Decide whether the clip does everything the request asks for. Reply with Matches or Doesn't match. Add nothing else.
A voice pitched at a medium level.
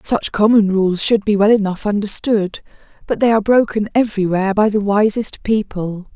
Doesn't match